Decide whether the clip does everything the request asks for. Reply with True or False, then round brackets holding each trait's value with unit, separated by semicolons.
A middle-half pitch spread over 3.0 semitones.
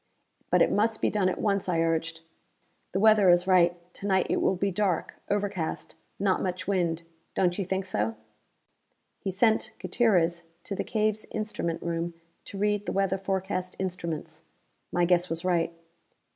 False (2.7 semitones)